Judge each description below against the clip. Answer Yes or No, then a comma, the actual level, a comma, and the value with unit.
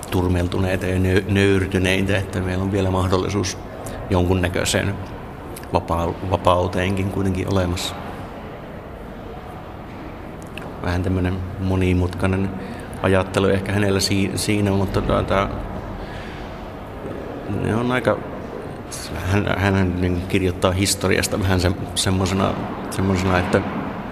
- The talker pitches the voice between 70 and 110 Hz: Yes, very low, 95 Hz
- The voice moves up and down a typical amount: No, narrow, 1.3 semitones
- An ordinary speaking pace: No, slow, 80 wpm